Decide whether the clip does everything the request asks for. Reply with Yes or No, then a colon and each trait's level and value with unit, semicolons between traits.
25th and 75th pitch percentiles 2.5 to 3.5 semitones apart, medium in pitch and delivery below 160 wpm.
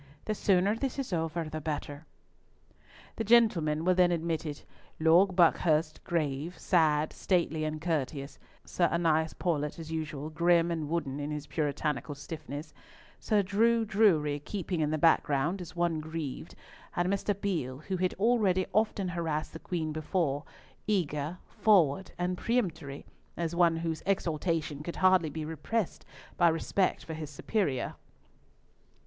Yes: average, 3.2 semitones; medium, 165 Hz; average, 145 wpm